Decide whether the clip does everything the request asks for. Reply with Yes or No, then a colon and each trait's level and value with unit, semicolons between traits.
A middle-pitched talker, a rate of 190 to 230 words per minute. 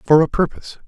Yes: medium, 145 Hz; fast, 205 wpm